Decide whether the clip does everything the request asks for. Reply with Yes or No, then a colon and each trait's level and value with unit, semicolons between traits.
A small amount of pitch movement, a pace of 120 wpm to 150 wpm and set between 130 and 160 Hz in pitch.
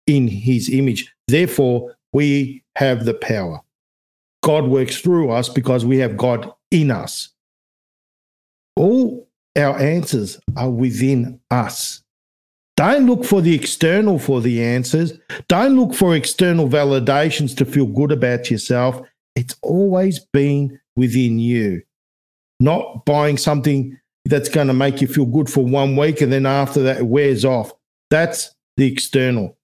No: average, 3.3 semitones; average, 140 wpm; low, 135 Hz